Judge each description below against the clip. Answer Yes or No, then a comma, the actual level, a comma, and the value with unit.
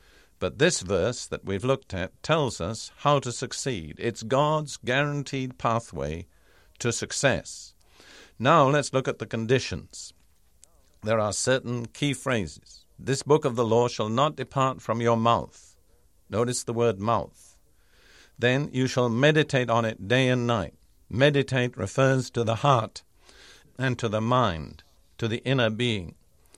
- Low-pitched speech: Yes, low, 120 Hz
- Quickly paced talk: No, average, 150 wpm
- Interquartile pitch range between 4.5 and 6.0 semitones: Yes, wide, 5.4 semitones